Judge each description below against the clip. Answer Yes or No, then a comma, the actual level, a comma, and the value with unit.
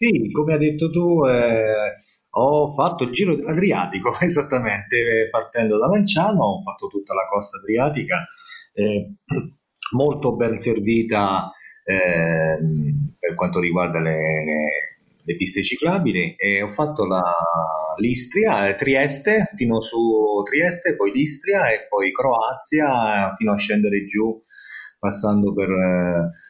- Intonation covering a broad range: Yes, wide, 7.8 semitones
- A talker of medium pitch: No, low, 110 Hz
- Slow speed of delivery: No, average, 125 wpm